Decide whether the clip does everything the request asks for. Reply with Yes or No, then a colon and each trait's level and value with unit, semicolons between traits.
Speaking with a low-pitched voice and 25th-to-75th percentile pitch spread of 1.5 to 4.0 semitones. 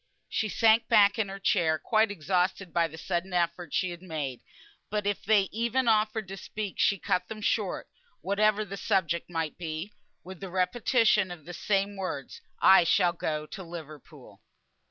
No: high, 190 Hz; average, 3.6 semitones